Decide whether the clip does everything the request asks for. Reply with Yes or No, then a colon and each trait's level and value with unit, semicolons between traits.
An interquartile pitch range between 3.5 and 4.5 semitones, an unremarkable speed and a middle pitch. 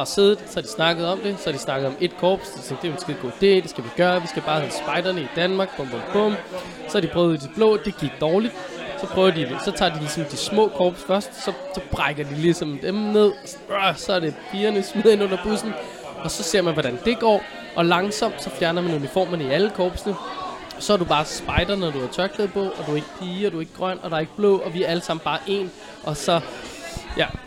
No: average, 4.0 semitones; fast, 260 wpm; medium, 180 Hz